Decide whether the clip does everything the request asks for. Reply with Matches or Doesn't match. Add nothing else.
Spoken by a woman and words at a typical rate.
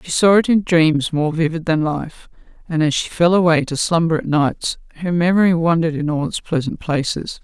Doesn't match